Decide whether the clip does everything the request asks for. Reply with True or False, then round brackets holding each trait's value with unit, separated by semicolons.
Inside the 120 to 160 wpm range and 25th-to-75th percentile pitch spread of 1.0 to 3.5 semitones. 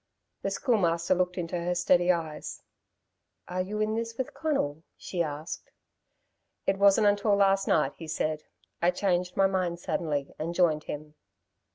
True (155 wpm; 3.2 semitones)